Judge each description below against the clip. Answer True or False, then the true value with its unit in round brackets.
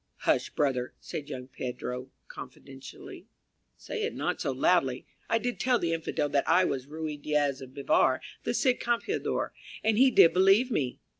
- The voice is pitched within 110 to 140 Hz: False (155 Hz)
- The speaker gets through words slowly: False (165 wpm)